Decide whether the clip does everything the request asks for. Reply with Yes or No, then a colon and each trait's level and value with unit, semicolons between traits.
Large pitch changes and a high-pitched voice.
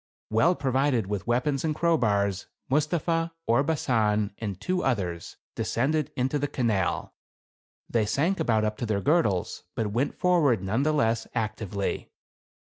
No: wide, 6.0 semitones; low, 120 Hz